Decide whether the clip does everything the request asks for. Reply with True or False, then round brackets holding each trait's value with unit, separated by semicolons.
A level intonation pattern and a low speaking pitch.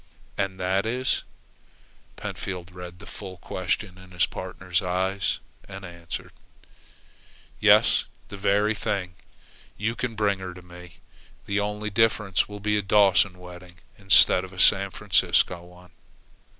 True (2.2 semitones; 95 Hz)